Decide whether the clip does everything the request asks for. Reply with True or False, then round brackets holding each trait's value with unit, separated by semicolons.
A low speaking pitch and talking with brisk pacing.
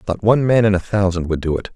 True (100 Hz; 310 wpm)